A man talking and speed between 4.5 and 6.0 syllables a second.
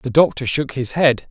Yes: male; 4.7 syllables/s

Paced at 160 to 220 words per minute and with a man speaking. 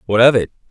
No: fast, 255 wpm; male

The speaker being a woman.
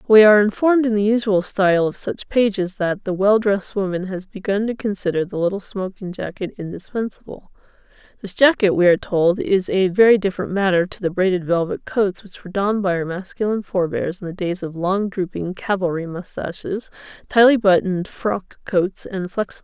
Yes: female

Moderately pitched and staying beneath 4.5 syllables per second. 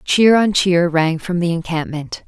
Yes: medium, 175 Hz; 4.2 syllables/s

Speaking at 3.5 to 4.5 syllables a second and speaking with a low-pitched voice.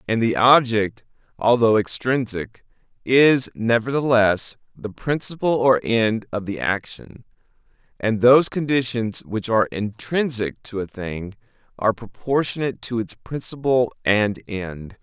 Yes: 4.2 syllables/s; low, 115 Hz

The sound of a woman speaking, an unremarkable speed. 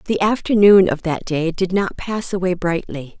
Yes: female; average, 190 wpm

